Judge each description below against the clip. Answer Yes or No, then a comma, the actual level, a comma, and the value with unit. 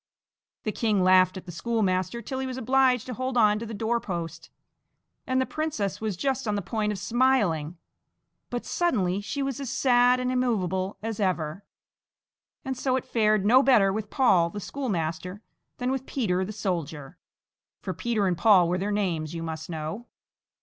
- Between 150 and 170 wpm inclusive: No, average, 180 wpm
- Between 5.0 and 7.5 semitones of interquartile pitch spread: Yes, wide, 5.4 semitones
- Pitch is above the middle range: Yes, high, 210 Hz